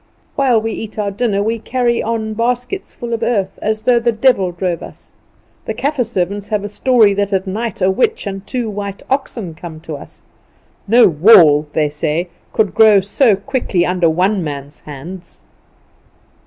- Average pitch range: Yes, average, 4.2 semitones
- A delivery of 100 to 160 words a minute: No, average, 180 wpm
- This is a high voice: Yes, high, 205 Hz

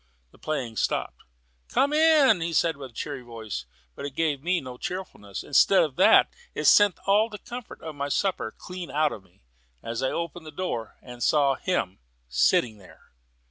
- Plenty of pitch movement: Yes, wide, 7.3 semitones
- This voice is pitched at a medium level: Yes, medium, 145 Hz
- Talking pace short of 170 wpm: No, average, 180 wpm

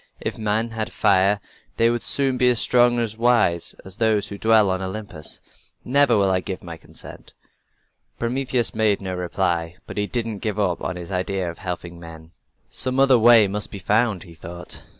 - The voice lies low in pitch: Yes, low, 105 Hz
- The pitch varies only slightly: No, average, 4.2 semitones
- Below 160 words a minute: No, average, 185 wpm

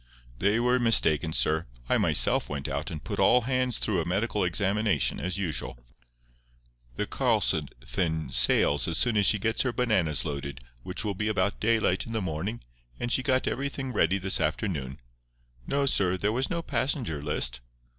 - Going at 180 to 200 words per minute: No, average, 170 wpm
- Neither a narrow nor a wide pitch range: No, wide, 6.7 semitones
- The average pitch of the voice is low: Yes, low, 100 Hz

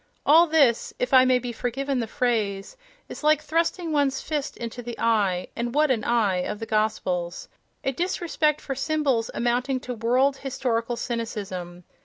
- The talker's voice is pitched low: No, high, 245 Hz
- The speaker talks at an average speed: Yes, average, 155 wpm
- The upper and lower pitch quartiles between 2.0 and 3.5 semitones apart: No, average, 4.0 semitones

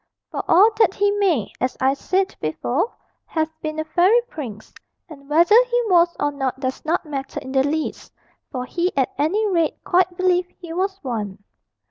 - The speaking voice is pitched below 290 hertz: No, very high, 320 Hz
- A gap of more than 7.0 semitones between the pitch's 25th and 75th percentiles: No, wide, 5.5 semitones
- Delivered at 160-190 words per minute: Yes, average, 180 wpm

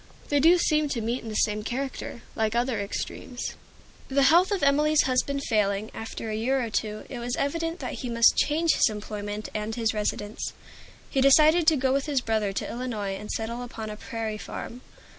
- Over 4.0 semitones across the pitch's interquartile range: Yes, average, 4.5 semitones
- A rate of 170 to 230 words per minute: Yes, average, 200 wpm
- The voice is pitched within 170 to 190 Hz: No, high, 240 Hz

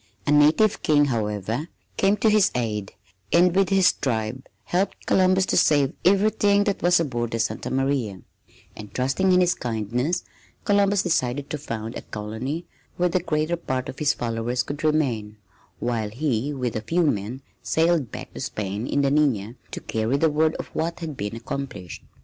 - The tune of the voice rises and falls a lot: Yes, wide, 6.9 semitones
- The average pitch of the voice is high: No, medium, 140 Hz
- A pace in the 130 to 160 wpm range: No, average, 175 wpm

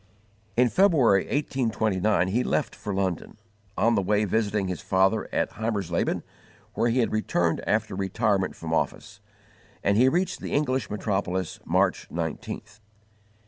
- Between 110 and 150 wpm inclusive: Yes, average, 140 wpm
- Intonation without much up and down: No, average, 3.7 semitones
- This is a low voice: Yes, low, 105 Hz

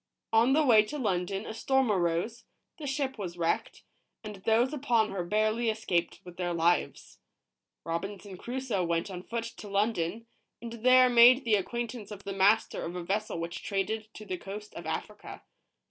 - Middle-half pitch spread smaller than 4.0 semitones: No, average, 4.3 semitones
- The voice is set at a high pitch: Yes, high, 215 Hz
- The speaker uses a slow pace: No, average, 175 wpm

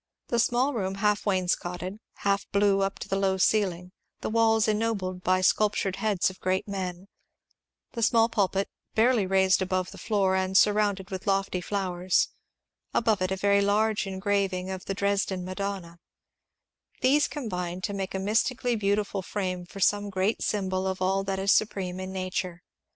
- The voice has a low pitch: No, high, 195 Hz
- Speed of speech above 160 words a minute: Yes, average, 170 wpm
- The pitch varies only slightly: Yes, narrow, 1.9 semitones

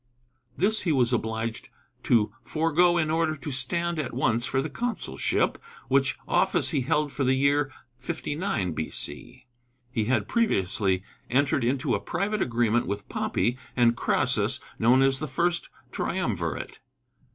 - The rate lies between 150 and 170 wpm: No, average, 140 wpm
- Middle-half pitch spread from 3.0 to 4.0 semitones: No, average, 5.3 semitones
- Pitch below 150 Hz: Yes, low, 135 Hz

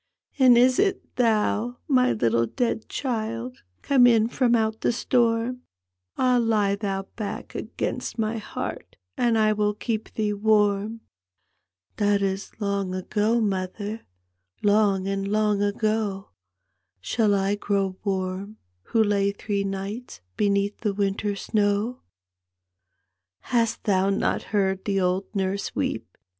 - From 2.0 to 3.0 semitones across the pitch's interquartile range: Yes, narrow, 2.4 semitones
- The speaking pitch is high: Yes, high, 205 Hz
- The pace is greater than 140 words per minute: No, slow, 135 wpm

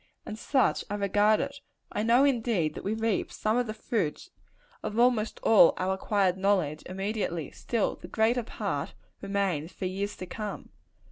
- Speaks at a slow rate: No, average, 165 wpm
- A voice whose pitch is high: Yes, high, 205 Hz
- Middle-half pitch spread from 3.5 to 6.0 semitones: No, average, 3.1 semitones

